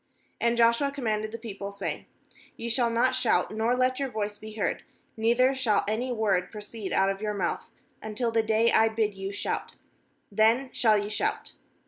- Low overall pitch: No, high, 220 Hz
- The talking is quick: No, average, 180 wpm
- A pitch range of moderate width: No, narrow, 2.2 semitones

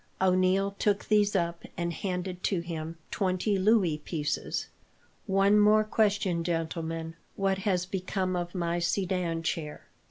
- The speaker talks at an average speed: No, slow, 130 wpm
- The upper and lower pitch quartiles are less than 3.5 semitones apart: Yes, narrow, 2.6 semitones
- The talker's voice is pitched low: No, medium, 185 Hz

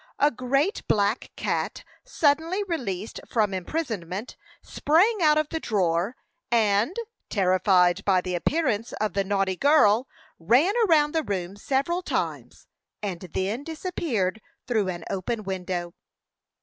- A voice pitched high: Yes, high, 220 Hz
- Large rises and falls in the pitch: Yes, wide, 8.0 semitones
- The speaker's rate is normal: No, slow, 125 wpm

